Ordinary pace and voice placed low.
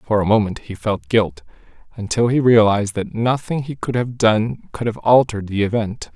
Yes: average, 195 wpm; low, 115 Hz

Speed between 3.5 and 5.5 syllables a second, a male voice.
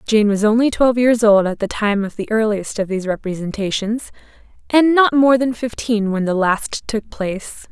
No: 5.0 syllables/s; female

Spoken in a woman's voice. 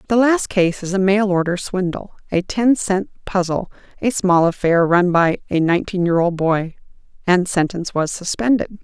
Yes: female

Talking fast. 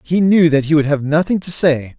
Yes: fast, 270 wpm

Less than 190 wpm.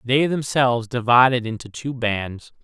Yes: slow, 135 wpm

